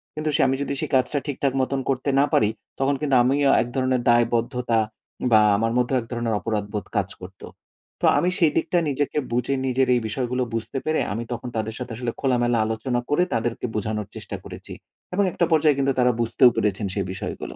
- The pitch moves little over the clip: No, average, 3.3 semitones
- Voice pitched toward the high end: No, low, 125 Hz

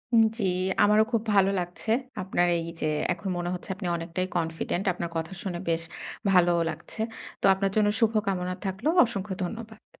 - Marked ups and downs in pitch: No, average, 3.1 semitones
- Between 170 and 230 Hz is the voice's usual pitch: Yes, medium, 185 Hz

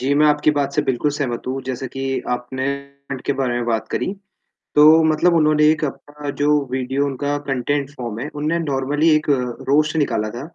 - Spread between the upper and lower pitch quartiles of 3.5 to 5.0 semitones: No, narrow, 2.4 semitones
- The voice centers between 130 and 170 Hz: Yes, medium, 140 Hz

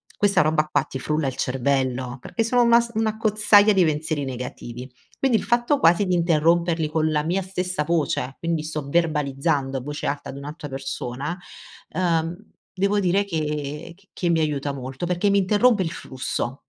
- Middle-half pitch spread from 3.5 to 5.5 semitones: Yes, average, 5.2 semitones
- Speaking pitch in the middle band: Yes, medium, 160 Hz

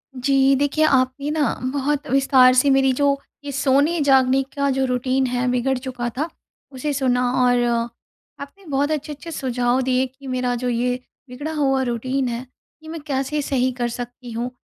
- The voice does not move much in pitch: Yes, narrow, 2.0 semitones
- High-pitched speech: Yes, very high, 265 Hz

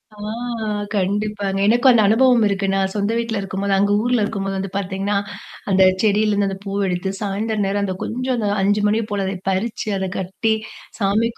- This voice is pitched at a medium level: No, high, 205 Hz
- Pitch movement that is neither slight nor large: No, narrow, 2.0 semitones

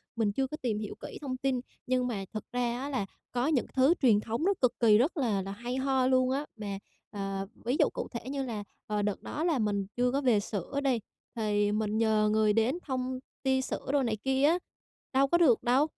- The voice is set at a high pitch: Yes, high, 245 Hz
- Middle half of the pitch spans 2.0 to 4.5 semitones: Yes, average, 3.9 semitones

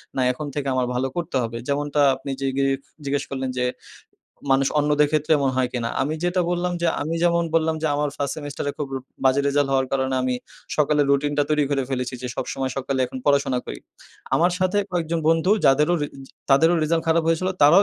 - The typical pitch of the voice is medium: Yes, medium, 145 Hz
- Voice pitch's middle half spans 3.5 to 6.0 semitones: No, average, 3.1 semitones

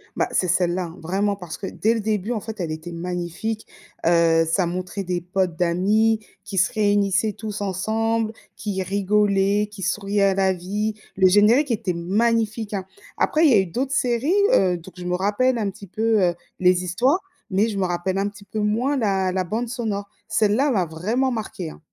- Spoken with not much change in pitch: No, average, 3.2 semitones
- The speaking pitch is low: No, high, 200 Hz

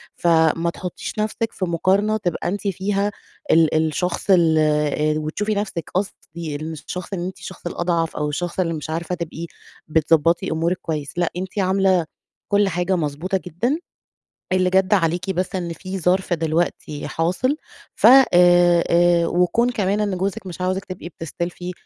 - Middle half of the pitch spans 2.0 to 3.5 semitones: Yes, narrow, 2.5 semitones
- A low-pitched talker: No, medium, 175 Hz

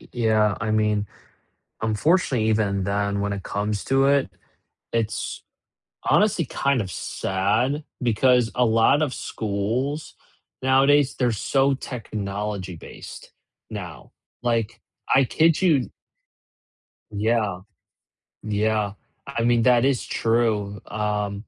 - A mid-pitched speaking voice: No, low, 110 Hz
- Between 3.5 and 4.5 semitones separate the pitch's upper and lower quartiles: Yes, average, 4.2 semitones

